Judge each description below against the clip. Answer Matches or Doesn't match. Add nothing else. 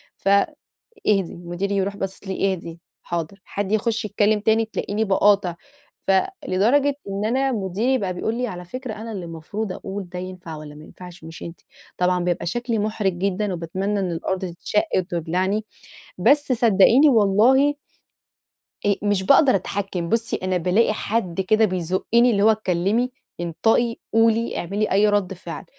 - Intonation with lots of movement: Doesn't match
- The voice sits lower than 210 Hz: Matches